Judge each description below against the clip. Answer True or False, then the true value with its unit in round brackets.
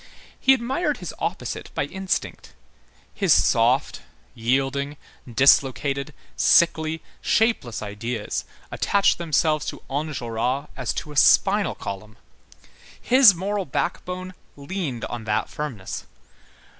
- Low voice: False (145 Hz)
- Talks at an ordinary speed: False (105 wpm)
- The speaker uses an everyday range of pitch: False (7.2 semitones)